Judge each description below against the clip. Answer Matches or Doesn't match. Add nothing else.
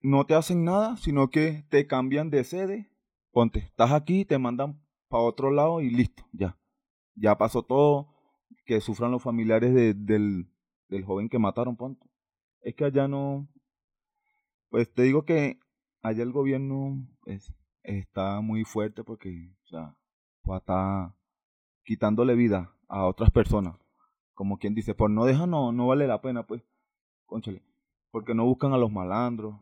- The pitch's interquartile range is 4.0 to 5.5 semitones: Matches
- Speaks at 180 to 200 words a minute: Doesn't match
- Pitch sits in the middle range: Doesn't match